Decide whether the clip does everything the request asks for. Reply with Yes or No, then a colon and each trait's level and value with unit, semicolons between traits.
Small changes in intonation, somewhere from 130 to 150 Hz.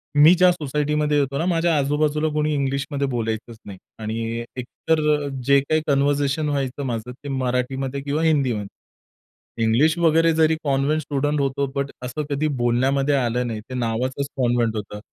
No: average, 3.2 semitones; medium, 140 Hz